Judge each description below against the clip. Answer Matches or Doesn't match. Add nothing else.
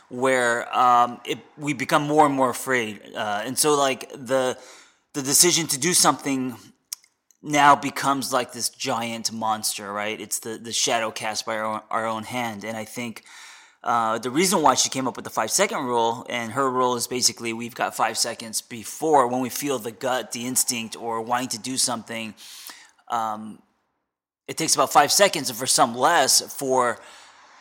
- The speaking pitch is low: Matches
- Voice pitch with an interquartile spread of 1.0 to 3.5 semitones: Matches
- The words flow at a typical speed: Matches